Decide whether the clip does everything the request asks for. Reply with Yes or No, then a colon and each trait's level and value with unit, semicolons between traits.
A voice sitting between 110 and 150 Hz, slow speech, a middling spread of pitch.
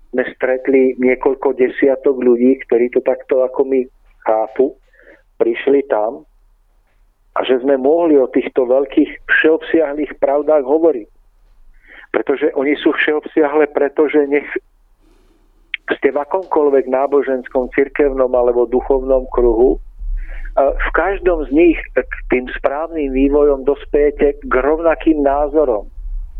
Yes: medium, 140 Hz; slow, 110 wpm; average, 3.4 semitones